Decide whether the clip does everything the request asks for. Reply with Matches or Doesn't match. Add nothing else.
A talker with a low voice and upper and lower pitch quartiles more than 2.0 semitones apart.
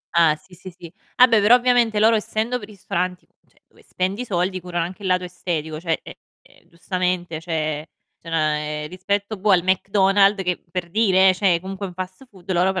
Doesn't match